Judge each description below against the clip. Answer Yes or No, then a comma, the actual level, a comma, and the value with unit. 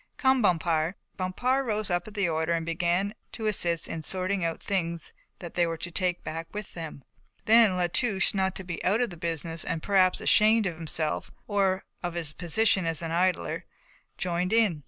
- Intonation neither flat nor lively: Yes, average, 3.2 semitones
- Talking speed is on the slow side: No, average, 195 wpm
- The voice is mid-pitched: Yes, medium, 180 Hz